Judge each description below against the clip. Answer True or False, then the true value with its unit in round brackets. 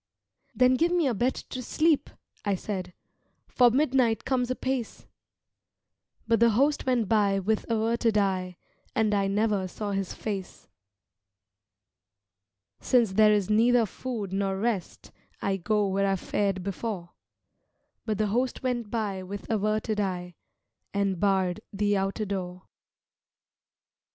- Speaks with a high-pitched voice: True (210 Hz)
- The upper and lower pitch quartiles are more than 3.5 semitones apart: False (3.2 semitones)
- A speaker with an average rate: False (130 wpm)